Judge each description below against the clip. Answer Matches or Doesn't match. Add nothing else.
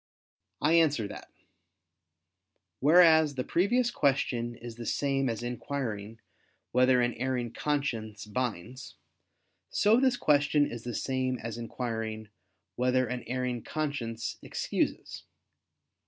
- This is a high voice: Doesn't match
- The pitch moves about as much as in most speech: Matches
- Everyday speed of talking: Doesn't match